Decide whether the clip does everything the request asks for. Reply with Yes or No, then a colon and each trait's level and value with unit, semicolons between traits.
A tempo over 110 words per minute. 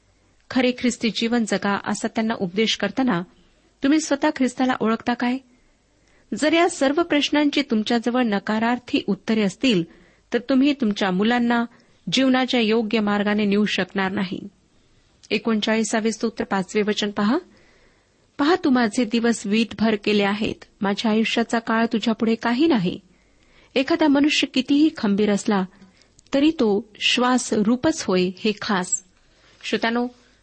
Yes: average, 120 wpm